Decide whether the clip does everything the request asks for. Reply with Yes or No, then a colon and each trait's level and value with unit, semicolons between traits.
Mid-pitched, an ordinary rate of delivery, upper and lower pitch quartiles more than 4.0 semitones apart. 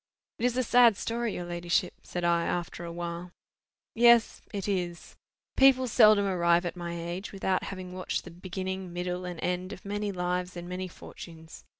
No: medium, 180 Hz; average, 180 wpm; narrow, 2.6 semitones